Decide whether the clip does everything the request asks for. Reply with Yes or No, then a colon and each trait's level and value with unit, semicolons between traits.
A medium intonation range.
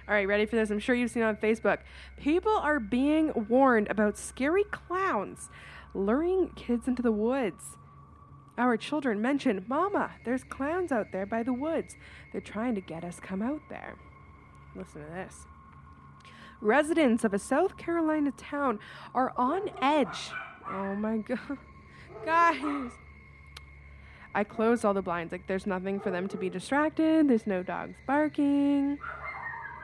No: wide, 6.6 semitones